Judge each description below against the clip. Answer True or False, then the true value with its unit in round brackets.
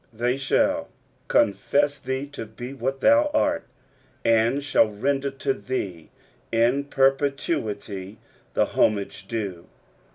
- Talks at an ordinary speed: False (110 wpm)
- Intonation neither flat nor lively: True (4.5 semitones)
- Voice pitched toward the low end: True (130 Hz)